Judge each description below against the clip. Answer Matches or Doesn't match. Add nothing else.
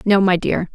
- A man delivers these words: Doesn't match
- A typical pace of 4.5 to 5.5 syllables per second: Matches